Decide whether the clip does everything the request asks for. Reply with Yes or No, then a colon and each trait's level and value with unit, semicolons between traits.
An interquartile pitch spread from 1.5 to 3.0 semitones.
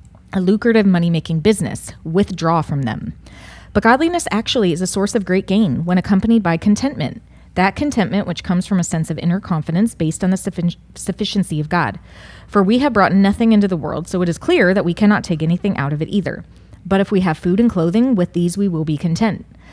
No: average, 3.7 semitones